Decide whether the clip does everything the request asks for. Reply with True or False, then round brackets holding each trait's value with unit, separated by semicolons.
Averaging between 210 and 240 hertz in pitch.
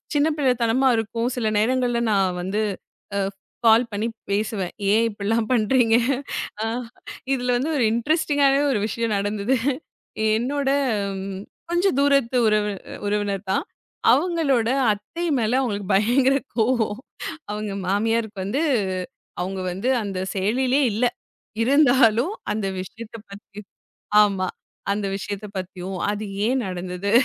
True (225 Hz)